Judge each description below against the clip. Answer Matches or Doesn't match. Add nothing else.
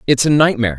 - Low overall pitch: Matches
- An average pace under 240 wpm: Matches